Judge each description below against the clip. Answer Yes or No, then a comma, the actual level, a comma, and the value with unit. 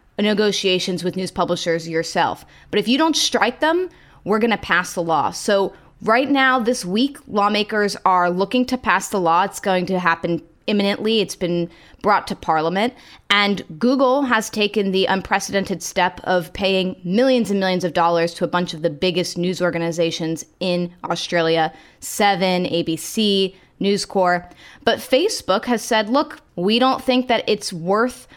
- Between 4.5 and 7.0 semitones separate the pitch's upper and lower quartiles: No, average, 3.8 semitones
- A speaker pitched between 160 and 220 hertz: Yes, high, 190 Hz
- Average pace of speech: Yes, average, 165 wpm